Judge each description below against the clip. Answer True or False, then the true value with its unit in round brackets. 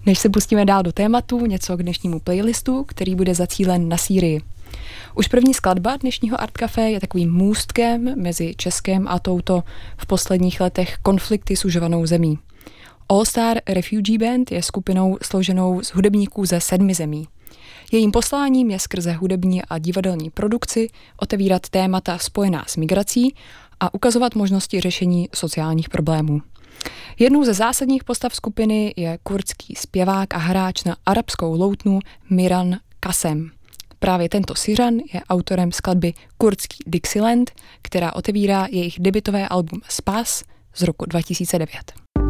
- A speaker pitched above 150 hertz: True (190 Hz)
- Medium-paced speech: True (140 wpm)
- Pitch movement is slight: False (3.3 semitones)